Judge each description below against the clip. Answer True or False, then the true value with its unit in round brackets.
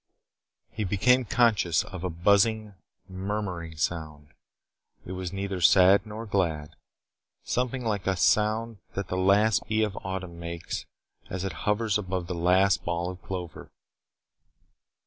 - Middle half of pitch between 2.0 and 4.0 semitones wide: True (3.2 semitones)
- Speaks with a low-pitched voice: True (95 Hz)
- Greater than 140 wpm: False (135 wpm)